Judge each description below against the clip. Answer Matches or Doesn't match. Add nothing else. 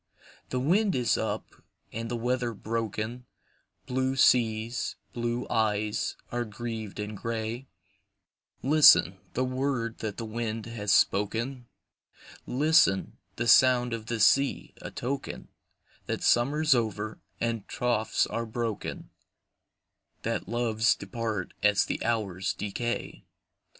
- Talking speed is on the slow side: Matches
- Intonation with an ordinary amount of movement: Doesn't match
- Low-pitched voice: Matches